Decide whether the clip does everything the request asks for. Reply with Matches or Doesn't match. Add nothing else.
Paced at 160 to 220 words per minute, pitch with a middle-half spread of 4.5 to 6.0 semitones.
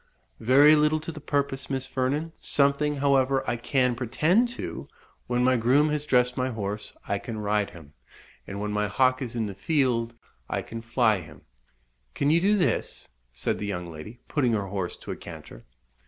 Matches